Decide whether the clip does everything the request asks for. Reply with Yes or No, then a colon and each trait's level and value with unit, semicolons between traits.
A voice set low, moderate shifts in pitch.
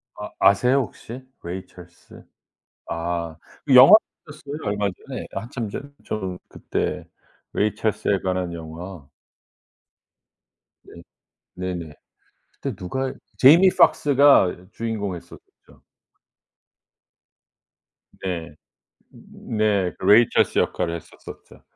No: low, 100 Hz; wide, 5.8 semitones